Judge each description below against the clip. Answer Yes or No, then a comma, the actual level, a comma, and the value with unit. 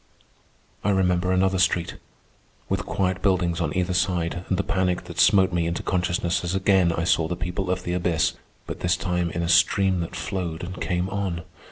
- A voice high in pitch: No, very low, 90 Hz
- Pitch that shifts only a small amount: Yes, narrow, 1.4 semitones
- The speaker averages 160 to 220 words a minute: Yes, average, 195 wpm